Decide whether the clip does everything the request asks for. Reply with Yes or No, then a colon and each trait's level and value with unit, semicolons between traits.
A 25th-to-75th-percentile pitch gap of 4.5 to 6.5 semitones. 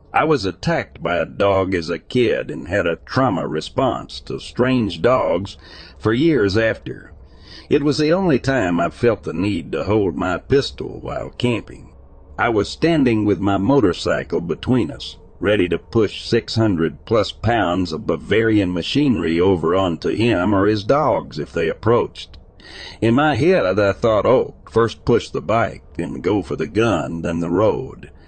Yes: average, 5.2 semitones